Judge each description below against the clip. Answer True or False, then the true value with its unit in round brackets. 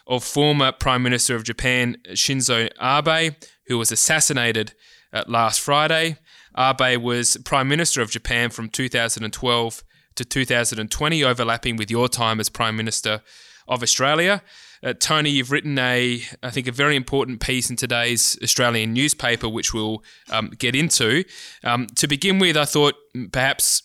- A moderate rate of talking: True (150 wpm)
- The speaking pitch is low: True (125 Hz)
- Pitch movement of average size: True (3.5 semitones)